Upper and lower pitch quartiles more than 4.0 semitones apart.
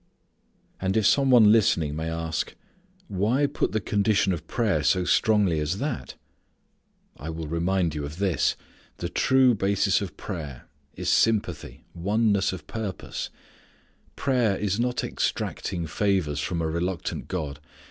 Yes: average, 4.7 semitones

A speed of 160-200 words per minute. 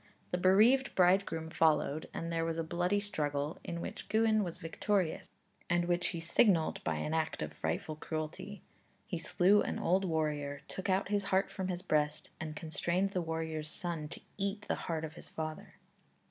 Yes: average, 180 wpm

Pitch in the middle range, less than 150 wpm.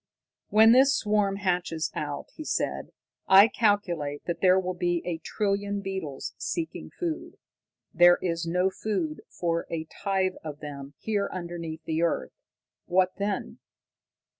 Yes: medium, 180 Hz; average, 140 wpm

